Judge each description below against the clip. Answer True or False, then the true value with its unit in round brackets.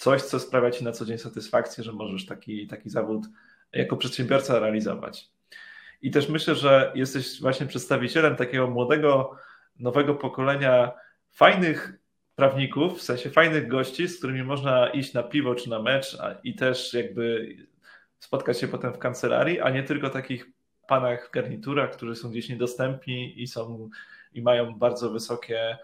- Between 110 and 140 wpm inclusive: False (160 wpm)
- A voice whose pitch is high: False (125 Hz)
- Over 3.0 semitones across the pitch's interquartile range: False (2.4 semitones)